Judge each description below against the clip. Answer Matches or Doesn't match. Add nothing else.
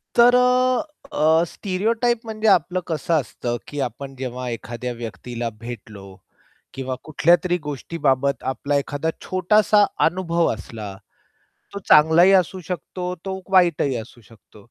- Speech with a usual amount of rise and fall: Doesn't match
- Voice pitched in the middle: Matches